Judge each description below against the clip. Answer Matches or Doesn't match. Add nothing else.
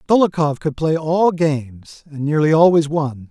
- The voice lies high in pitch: Doesn't match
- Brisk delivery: Doesn't match